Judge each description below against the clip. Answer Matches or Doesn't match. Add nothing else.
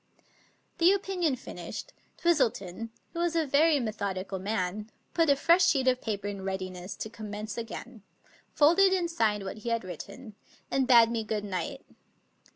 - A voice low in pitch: Doesn't match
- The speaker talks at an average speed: Matches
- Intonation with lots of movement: Matches